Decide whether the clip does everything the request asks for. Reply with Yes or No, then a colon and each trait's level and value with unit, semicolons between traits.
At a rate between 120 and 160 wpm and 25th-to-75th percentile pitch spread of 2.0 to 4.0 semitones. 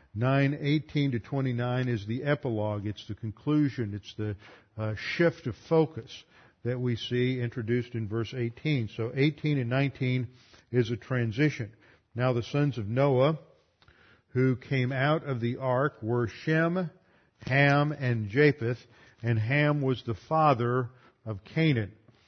Yes: average, 145 wpm; average, 3.6 semitones